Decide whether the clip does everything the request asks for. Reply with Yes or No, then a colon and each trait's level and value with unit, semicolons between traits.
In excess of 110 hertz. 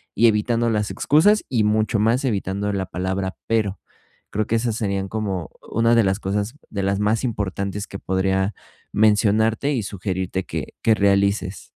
No: low, 105 Hz